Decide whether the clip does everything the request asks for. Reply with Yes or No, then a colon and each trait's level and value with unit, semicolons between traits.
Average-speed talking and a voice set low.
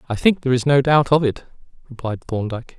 No: fast, 215 wpm; low, 130 Hz